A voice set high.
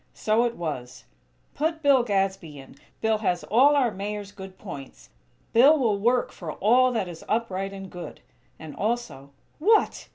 Yes: high, 210 Hz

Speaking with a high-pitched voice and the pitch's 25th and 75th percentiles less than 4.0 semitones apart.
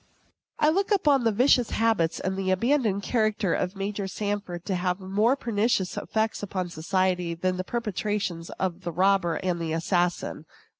Yes: high, 195 Hz; average, 3.5 semitones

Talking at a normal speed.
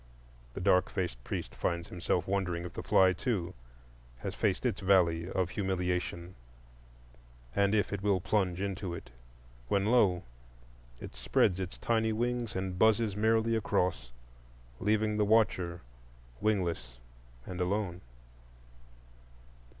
No: slow, 120 wpm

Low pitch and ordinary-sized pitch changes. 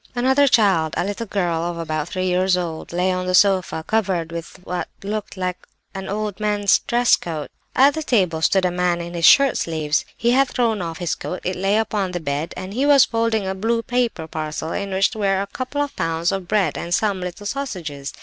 No: high, 190 Hz; average, 4.2 semitones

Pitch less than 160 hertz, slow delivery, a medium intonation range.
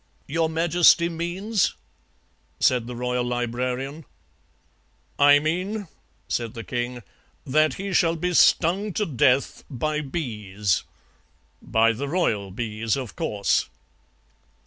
No: medium, 140 Hz; slow, 115 wpm; wide, 5.8 semitones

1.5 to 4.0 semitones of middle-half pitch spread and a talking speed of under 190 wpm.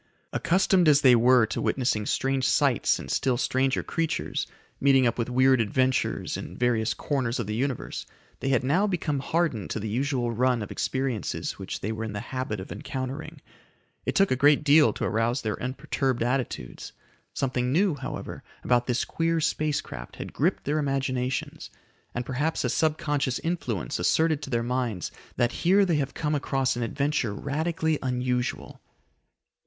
Yes: average, 3.5 semitones; average, 170 wpm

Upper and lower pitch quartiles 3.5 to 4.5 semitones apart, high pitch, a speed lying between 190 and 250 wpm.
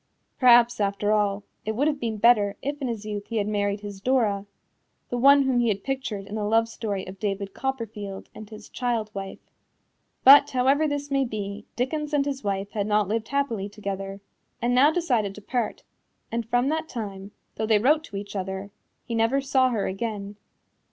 Yes: average, 4.2 semitones; high, 220 Hz; average, 195 wpm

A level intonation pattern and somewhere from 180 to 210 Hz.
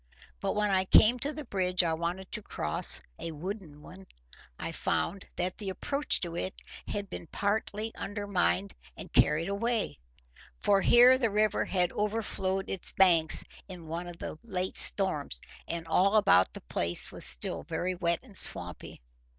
No: average, 3.7 semitones; medium, 185 Hz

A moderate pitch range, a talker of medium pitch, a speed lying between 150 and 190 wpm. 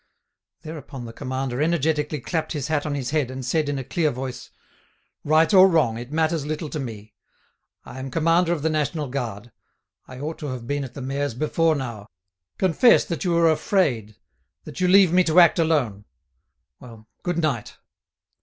Yes: average, 4.2 semitones; medium, 150 Hz; average, 180 wpm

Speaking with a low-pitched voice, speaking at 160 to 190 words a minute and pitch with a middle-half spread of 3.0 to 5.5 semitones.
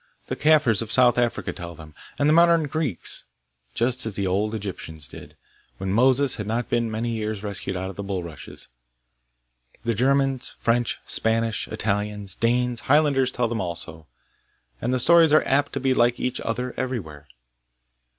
Yes: low, 115 Hz; average, 165 wpm; average, 4.5 semitones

